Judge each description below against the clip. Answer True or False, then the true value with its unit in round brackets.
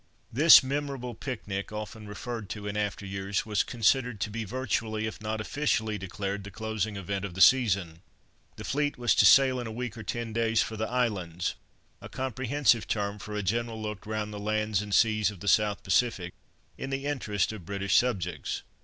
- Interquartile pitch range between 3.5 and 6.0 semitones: False (3.0 semitones)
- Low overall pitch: True (110 Hz)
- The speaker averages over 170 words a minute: True (190 wpm)